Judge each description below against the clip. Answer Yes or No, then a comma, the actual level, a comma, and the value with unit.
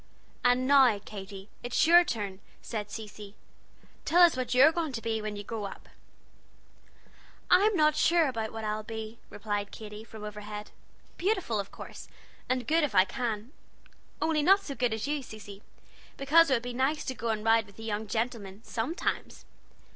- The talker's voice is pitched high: Yes, high, 225 Hz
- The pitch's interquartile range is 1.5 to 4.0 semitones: No, average, 4.8 semitones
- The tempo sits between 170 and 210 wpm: Yes, average, 175 wpm